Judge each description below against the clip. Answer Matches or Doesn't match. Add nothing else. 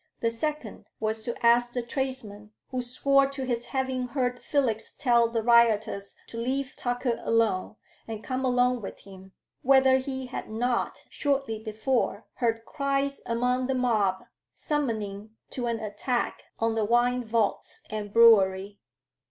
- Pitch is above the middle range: Matches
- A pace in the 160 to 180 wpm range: Doesn't match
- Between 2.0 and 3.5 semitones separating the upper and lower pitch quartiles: Matches